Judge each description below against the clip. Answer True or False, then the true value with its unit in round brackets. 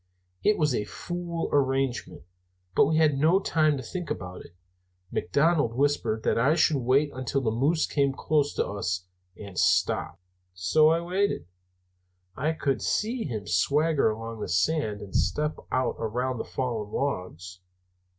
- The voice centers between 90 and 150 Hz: True (135 Hz)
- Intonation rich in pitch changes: True (6.1 semitones)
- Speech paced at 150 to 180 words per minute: True (155 wpm)